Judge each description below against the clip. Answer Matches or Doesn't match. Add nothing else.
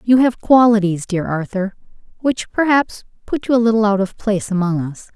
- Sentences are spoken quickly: Doesn't match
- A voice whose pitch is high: Matches